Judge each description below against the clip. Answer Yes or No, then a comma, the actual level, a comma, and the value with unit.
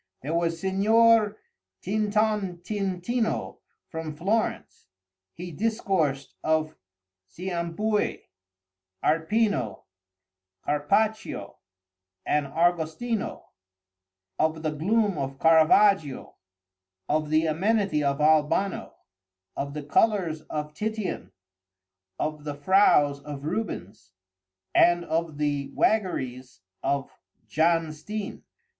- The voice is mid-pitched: Yes, medium, 160 Hz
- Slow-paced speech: Yes, slow, 85 wpm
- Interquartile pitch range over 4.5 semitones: Yes, wide, 5.5 semitones